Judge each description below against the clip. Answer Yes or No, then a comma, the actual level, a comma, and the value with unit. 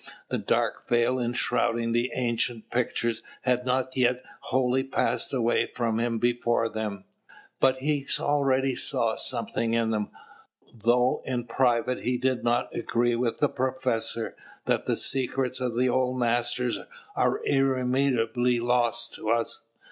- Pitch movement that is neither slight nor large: No, narrow, 1.6 semitones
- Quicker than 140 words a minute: No, slow, 135 wpm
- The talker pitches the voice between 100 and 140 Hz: Yes, low, 120 Hz